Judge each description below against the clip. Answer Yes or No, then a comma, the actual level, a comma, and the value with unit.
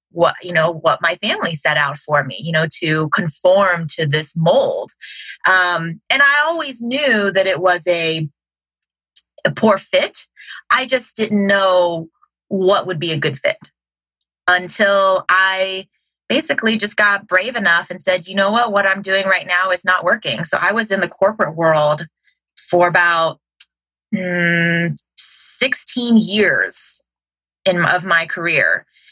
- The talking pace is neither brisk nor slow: Yes, average, 155 wpm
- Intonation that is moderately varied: Yes, average, 3.5 semitones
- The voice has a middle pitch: Yes, medium, 180 Hz